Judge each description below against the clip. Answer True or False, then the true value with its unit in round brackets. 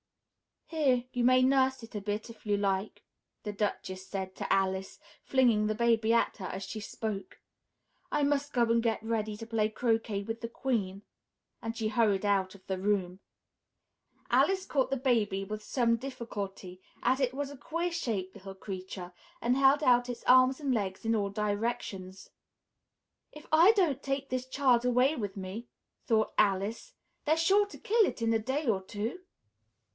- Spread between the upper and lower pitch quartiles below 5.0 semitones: True (4.5 semitones)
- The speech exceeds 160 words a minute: True (175 wpm)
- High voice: True (225 Hz)